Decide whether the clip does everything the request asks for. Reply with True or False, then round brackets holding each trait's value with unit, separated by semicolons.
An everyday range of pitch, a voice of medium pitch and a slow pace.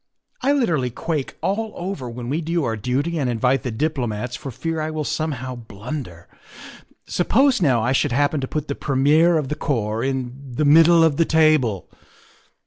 False (4.4 semitones; 145 Hz; 185 wpm)